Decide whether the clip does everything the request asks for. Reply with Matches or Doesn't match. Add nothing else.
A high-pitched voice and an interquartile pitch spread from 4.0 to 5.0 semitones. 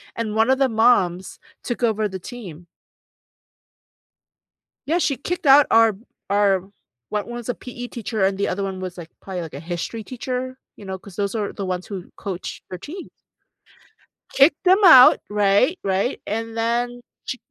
Matches